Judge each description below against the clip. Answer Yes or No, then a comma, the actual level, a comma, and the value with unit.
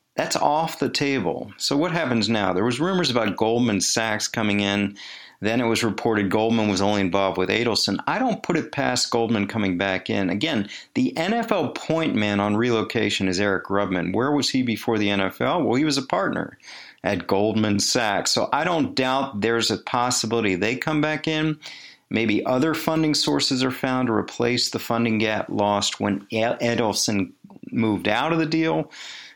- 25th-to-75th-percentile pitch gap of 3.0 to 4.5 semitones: Yes, average, 4.2 semitones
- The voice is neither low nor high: No, low, 115 Hz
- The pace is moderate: Yes, average, 180 wpm